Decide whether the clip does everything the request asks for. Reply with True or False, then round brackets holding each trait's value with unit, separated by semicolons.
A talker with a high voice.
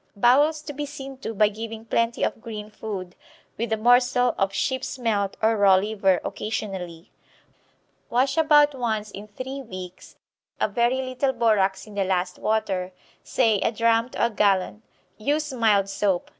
True (220 Hz)